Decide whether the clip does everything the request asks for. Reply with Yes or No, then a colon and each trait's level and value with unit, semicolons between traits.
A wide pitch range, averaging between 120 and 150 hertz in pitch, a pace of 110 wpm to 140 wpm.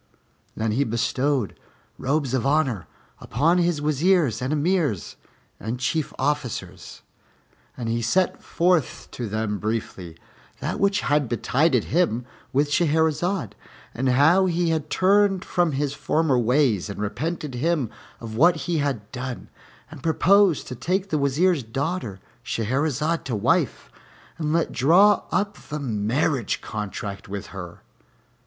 Yes: wide, 6.2 semitones; medium, 140 Hz; slow, 135 wpm